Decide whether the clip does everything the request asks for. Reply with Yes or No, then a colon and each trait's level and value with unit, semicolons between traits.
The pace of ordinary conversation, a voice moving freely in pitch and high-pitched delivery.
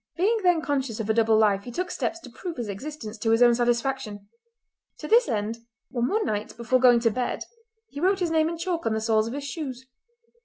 No: fast, 230 wpm; wide, 6.4 semitones; high, 245 Hz